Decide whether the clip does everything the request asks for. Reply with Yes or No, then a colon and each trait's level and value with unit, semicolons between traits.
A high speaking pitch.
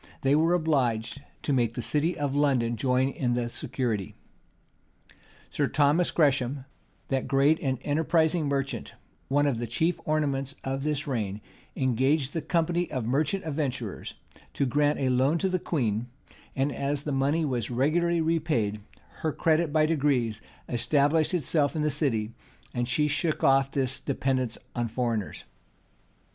No: medium, 140 Hz